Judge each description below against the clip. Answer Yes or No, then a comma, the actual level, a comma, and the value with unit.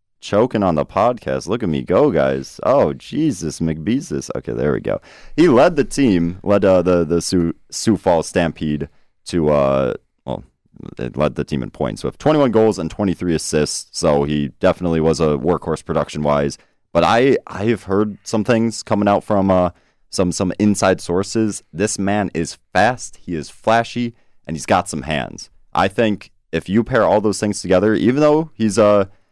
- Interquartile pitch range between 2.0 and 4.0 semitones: No, average, 4.9 semitones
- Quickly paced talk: No, average, 185 wpm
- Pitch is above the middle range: No, very low, 95 Hz